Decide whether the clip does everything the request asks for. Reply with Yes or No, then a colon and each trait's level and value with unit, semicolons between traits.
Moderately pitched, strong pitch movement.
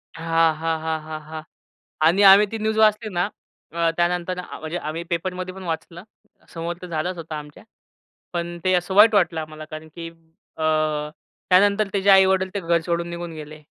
No: medium, 170 Hz; average, 2.7 semitones